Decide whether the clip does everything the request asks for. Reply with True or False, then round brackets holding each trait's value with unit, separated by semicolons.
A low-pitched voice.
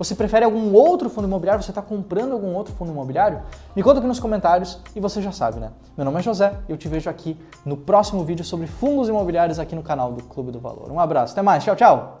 False (185 Hz)